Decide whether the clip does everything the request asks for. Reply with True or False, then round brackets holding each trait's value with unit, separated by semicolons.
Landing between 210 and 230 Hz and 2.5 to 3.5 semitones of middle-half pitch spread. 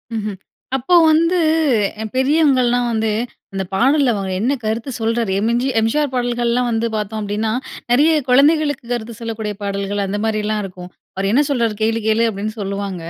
True (225 Hz; 3.2 semitones)